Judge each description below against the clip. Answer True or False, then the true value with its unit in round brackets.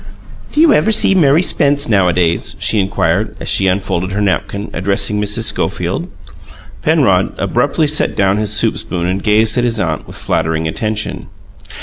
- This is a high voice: False (105 Hz)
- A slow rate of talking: False (160 wpm)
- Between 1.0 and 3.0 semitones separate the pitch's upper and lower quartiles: False (3.7 semitones)